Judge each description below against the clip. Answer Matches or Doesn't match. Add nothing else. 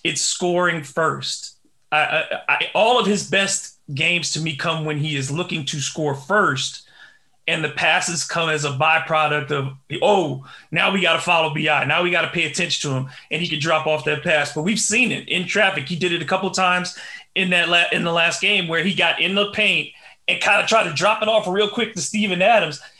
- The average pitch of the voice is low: Doesn't match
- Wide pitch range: Doesn't match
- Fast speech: Matches